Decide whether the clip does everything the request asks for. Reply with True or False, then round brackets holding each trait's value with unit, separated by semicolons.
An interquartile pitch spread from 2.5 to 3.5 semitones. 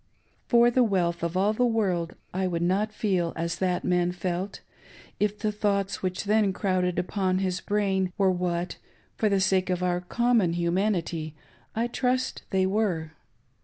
True (2.8 semitones)